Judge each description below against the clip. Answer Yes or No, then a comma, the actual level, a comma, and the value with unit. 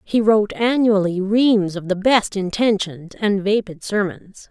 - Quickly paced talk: No, average, 145 wpm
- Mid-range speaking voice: No, high, 205 Hz